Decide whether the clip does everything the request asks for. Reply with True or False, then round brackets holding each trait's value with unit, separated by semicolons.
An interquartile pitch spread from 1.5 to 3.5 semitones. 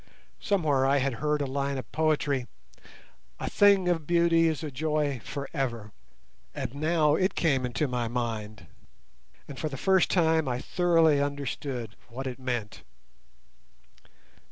False (3.9 semitones)